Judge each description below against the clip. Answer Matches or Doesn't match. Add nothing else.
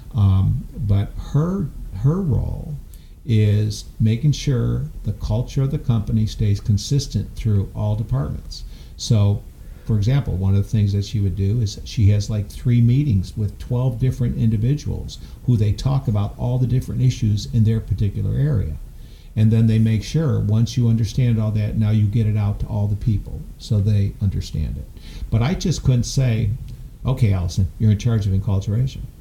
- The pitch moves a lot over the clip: Doesn't match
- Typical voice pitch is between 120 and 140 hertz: Doesn't match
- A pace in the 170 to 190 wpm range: Matches